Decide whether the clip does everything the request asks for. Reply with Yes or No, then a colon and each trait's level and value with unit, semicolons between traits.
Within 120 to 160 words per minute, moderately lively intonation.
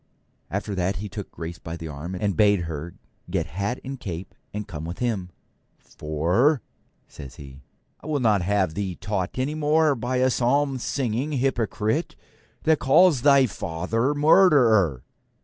No: average, 155 wpm; wide, 7.2 semitones